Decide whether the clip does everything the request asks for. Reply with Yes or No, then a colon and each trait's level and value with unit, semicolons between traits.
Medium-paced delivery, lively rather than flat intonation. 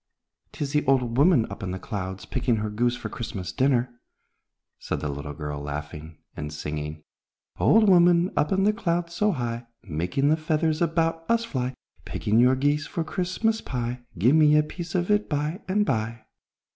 Yes: average, 180 wpm; wide, 8.4 semitones